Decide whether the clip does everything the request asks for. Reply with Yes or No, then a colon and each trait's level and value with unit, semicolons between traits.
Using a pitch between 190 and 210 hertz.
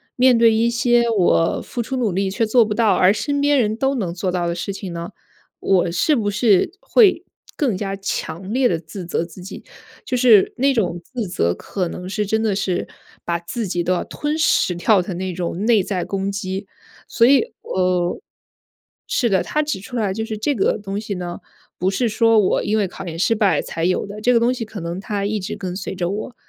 Yes: high, 200 Hz